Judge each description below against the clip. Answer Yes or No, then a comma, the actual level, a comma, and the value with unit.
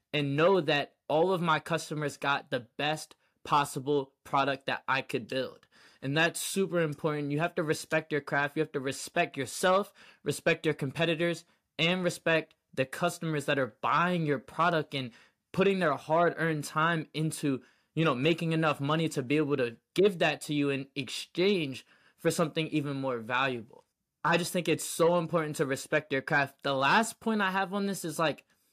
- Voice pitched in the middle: Yes, medium, 155 Hz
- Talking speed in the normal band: Yes, average, 185 wpm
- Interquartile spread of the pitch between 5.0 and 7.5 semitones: No, average, 3.0 semitones